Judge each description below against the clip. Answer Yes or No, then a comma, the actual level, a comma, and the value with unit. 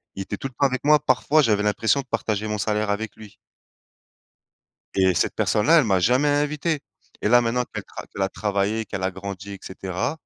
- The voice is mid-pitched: No, low, 110 Hz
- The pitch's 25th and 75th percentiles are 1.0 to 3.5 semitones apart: No, average, 5.0 semitones